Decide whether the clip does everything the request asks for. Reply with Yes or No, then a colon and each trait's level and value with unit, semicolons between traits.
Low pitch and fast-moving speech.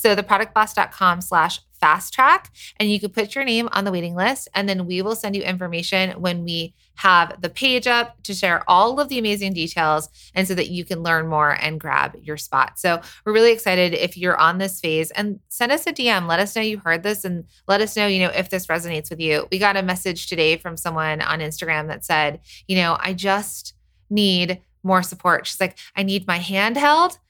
No: medium, 185 Hz; fast, 225 wpm